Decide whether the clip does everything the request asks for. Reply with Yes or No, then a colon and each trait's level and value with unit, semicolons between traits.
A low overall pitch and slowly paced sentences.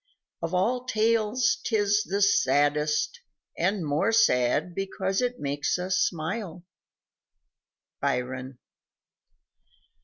No: medium, 185 Hz; slow, 90 wpm